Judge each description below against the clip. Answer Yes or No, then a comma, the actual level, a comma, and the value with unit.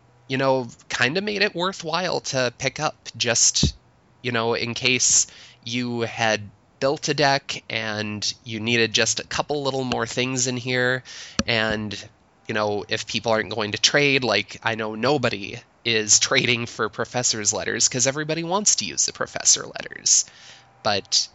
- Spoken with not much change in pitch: No, average, 3.4 semitones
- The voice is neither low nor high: No, low, 120 Hz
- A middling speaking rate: Yes, average, 165 wpm